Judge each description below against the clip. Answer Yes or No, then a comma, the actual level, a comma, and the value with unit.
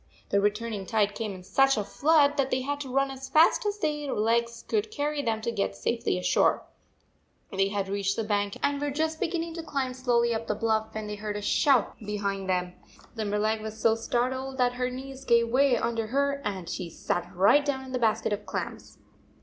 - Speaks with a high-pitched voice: Yes, high, 235 Hz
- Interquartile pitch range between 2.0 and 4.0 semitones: No, average, 4.7 semitones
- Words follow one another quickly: Yes, fast, 215 wpm